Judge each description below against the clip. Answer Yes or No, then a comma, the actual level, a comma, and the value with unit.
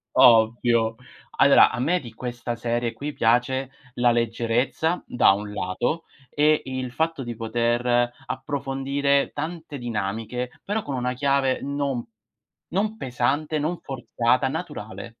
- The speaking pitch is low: Yes, low, 125 Hz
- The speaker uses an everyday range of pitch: Yes, average, 3.2 semitones